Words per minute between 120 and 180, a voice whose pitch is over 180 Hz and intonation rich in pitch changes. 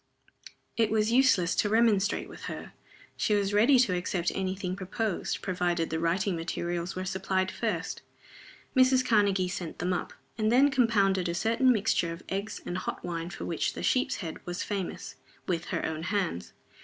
No: average, 175 wpm; high, 190 Hz; average, 3.8 semitones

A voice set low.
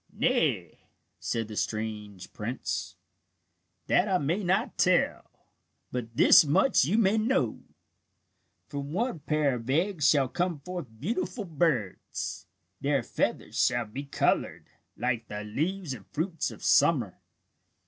No: medium, 145 Hz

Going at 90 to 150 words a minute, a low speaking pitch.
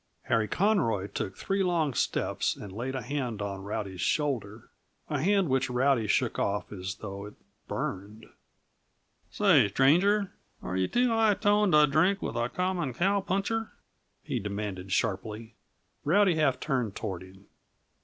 Yes: average, 145 wpm; low, 130 Hz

